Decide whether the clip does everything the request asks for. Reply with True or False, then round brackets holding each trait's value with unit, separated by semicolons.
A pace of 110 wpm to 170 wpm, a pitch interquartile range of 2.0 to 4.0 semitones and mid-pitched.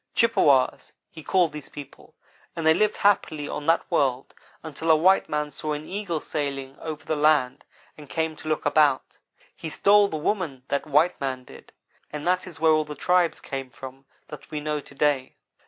False (190 wpm; 2.5 semitones; 150 Hz)